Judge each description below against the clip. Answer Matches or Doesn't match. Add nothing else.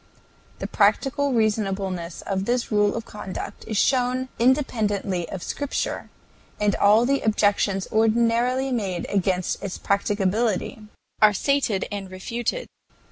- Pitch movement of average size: Matches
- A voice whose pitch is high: Matches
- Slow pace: Matches